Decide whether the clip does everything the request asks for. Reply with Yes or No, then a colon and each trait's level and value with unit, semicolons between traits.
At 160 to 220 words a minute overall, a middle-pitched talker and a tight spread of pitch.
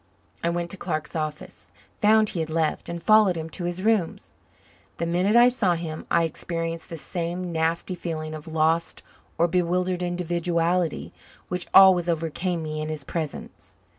Yes: average, 165 wpm; medium, 170 Hz; narrow, 1.9 semitones